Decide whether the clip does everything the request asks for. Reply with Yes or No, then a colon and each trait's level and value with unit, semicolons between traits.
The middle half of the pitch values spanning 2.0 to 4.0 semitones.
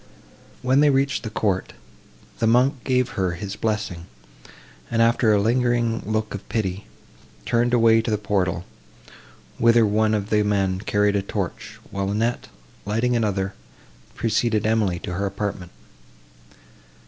Yes: average, 2.8 semitones